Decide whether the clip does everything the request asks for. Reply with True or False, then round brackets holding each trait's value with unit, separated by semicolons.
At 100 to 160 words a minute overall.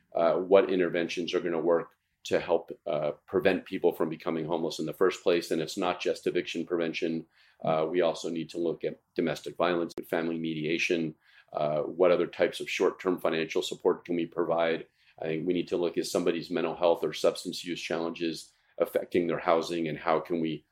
False (205 wpm)